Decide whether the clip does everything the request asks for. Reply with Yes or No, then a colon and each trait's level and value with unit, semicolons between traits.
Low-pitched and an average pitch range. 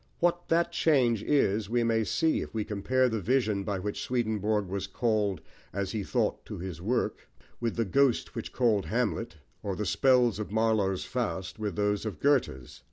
Yes: low, 110 Hz; average, 3.5 semitones